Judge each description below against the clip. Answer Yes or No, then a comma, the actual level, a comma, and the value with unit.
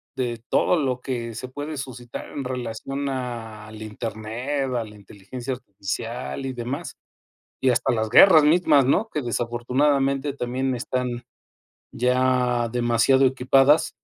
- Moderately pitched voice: No, low, 125 Hz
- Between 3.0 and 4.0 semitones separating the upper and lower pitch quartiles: No, narrow, 2.5 semitones